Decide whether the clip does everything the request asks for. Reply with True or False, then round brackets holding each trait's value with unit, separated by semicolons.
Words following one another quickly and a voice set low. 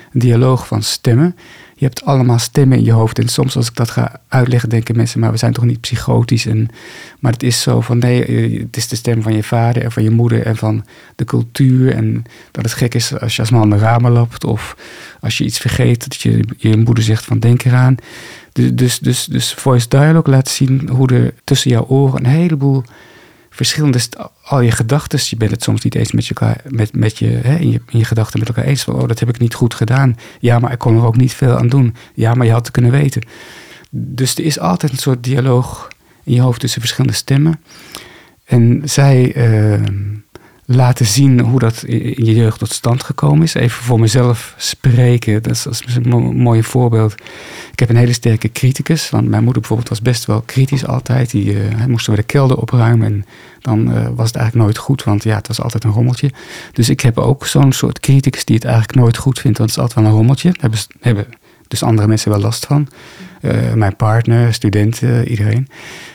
True (225 wpm; 120 Hz)